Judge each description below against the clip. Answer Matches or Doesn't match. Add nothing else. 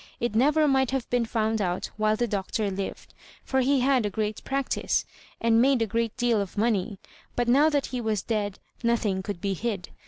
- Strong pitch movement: Doesn't match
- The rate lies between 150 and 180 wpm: Doesn't match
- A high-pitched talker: Matches